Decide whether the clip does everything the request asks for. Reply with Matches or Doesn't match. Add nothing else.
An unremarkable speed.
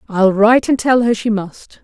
Doesn't match